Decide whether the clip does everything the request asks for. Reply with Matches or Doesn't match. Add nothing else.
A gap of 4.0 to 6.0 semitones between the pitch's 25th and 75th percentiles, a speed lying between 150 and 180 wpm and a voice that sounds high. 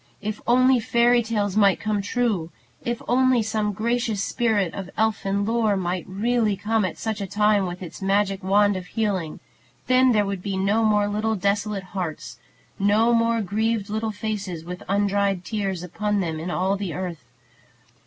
Doesn't match